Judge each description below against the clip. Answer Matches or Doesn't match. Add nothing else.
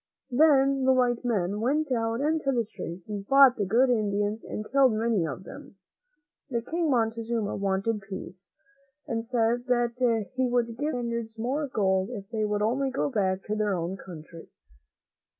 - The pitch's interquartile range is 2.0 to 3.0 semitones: Doesn't match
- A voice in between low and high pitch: Doesn't match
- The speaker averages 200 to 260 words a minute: Doesn't match